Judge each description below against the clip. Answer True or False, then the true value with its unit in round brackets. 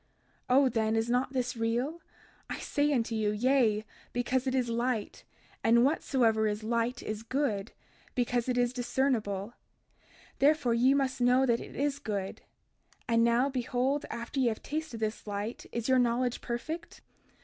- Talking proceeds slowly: False (160 wpm)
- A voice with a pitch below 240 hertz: False (245 Hz)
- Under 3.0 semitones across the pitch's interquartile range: True (2.6 semitones)